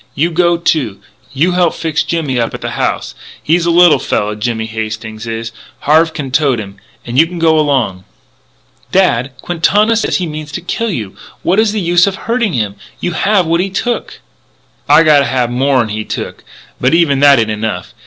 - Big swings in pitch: Yes, wide, 6.8 semitones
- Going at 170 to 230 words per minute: Yes, average, 195 wpm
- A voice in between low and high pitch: Yes, medium, 150 Hz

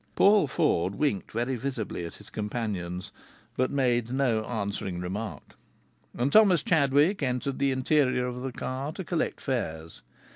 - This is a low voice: Yes, low, 125 Hz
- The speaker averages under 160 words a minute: Yes, average, 145 wpm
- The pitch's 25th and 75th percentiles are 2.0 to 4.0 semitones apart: No, average, 4.8 semitones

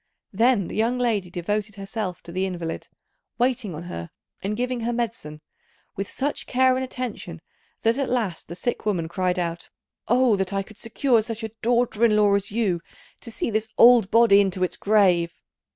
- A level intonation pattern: No, average, 4.3 semitones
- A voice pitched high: Yes, high, 210 Hz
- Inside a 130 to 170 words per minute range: No, average, 185 wpm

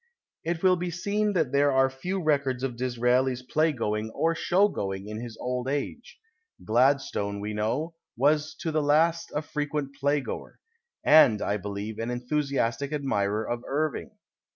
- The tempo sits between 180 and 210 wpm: No, average, 160 wpm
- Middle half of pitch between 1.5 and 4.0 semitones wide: No, average, 4.7 semitones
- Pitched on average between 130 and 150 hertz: Yes, low, 135 Hz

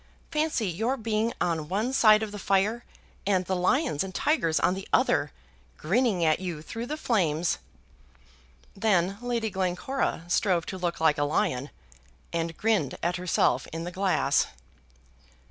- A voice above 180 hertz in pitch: Yes, high, 190 Hz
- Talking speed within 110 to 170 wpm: Yes, average, 150 wpm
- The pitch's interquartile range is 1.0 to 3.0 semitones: No, average, 4.9 semitones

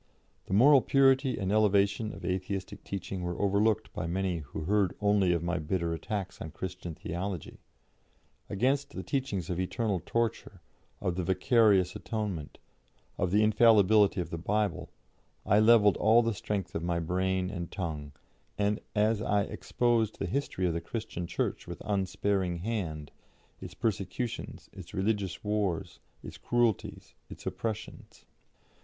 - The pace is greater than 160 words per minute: No, average, 145 wpm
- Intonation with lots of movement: No, average, 3.3 semitones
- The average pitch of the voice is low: Yes, low, 100 Hz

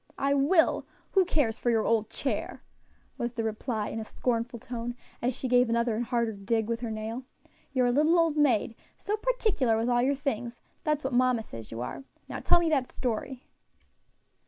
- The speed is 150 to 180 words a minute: No, average, 195 wpm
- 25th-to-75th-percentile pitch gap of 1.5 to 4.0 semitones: Yes, average, 3.5 semitones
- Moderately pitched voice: No, high, 245 Hz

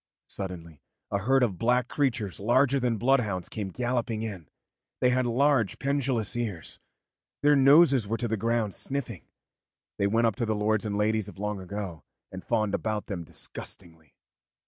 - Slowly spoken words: No, average, 165 wpm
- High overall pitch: No, low, 110 Hz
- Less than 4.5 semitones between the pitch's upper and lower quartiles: Yes, average, 3.9 semitones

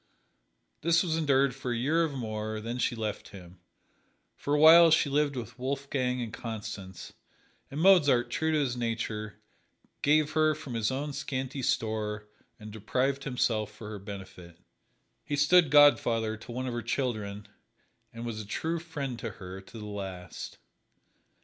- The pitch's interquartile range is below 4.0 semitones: No, average, 5.0 semitones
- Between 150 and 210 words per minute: Yes, average, 160 wpm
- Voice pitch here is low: Yes, low, 120 Hz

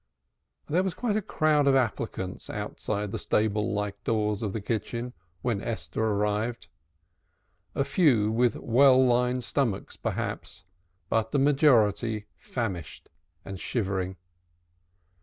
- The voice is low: Yes, low, 115 Hz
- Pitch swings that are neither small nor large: Yes, average, 3.7 semitones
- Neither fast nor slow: No, slow, 120 wpm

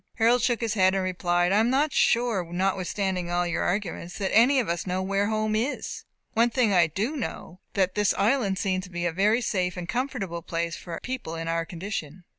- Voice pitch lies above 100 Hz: Yes, high, 190 Hz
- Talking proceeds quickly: Yes, fast, 215 wpm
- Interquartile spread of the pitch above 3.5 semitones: Yes, average, 4.2 semitones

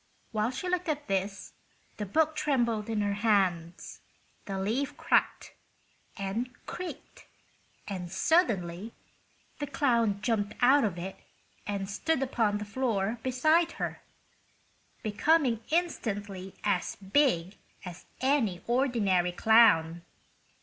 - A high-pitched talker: Yes, high, 215 Hz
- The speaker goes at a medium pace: No, slow, 115 wpm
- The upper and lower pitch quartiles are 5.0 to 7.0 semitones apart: Yes, wide, 5.4 semitones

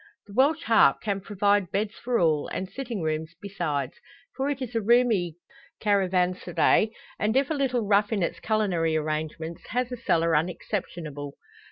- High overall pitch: Yes, high, 200 Hz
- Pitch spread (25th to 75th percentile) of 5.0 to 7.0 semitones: Yes, wide, 5.6 semitones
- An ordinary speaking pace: Yes, average, 160 wpm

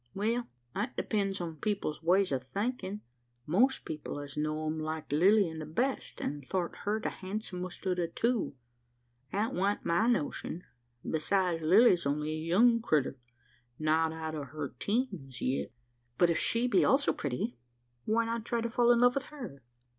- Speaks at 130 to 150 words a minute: No, average, 170 wpm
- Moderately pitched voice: Yes, medium, 180 Hz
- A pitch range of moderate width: No, wide, 6.3 semitones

